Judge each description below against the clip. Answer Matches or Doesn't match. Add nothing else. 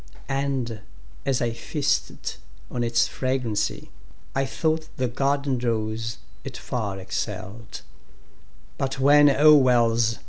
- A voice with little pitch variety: Doesn't match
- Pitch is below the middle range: Matches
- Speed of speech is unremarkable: Doesn't match